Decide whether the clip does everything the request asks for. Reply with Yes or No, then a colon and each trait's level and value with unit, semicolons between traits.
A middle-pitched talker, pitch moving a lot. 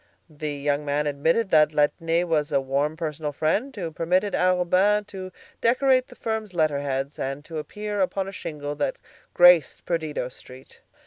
No: medium, 160 Hz; average, 4.2 semitones